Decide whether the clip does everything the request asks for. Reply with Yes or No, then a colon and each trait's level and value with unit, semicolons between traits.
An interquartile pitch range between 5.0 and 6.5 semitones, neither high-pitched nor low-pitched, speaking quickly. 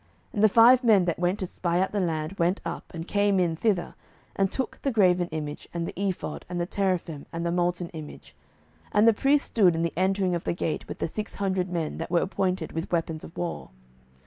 No: average, 2.8 semitones; medium, 180 Hz; fast, 230 wpm